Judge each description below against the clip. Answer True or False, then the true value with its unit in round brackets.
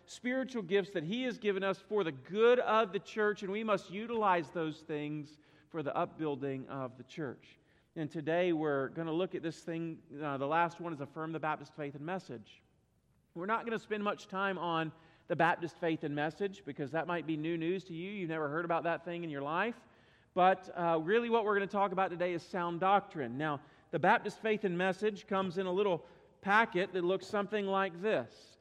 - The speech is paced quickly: True (220 wpm)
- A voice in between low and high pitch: True (175 Hz)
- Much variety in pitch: False (4.2 semitones)